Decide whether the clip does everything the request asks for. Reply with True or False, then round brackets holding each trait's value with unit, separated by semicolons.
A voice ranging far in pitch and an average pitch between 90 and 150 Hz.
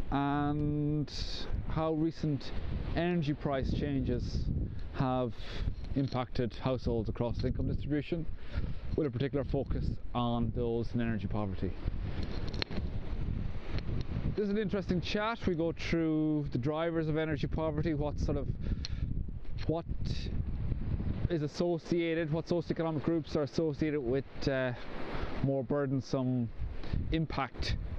True (6.2 semitones; 135 Hz)